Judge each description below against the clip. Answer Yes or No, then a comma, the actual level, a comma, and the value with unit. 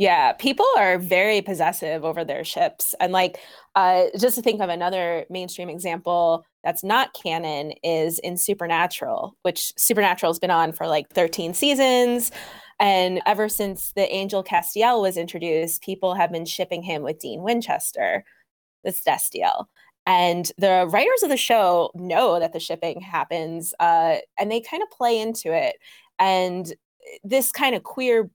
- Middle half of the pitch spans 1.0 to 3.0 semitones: No, average, 5.1 semitones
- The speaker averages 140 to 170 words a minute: Yes, average, 155 wpm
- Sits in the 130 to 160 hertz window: No, medium, 185 Hz